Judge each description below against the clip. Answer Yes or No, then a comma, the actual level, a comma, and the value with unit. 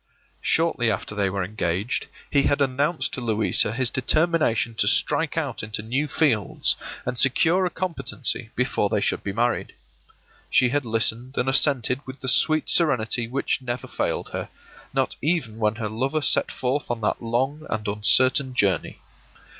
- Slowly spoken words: No, average, 160 wpm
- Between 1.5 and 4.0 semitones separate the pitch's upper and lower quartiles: No, average, 4.5 semitones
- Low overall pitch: Yes, low, 125 Hz